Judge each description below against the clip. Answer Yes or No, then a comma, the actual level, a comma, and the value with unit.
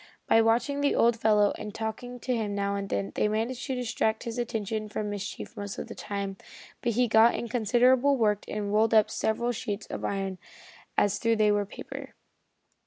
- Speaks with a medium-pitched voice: No, high, 220 Hz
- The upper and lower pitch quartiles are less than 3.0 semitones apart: Yes, narrow, 2.5 semitones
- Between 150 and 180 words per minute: No, average, 195 wpm